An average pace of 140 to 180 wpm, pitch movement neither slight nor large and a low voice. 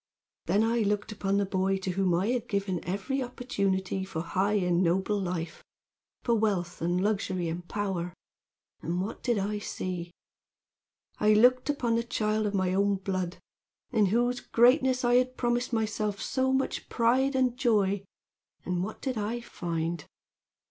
No: average, 160 wpm; average, 4.2 semitones; high, 205 Hz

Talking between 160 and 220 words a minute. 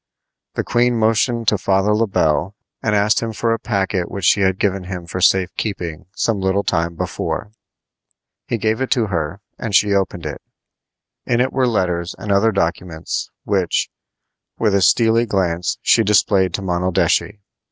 Yes: average, 170 wpm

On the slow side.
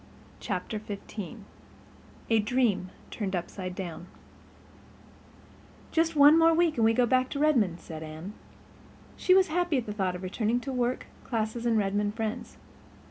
No: average, 150 wpm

